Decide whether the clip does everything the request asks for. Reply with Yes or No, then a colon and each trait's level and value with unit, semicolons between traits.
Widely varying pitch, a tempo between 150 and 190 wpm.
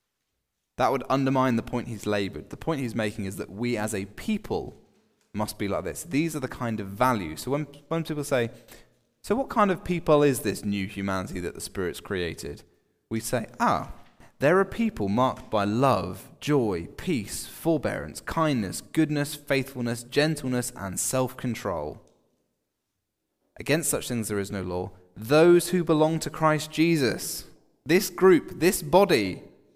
Yes: wide, 6.6 semitones; average, 160 wpm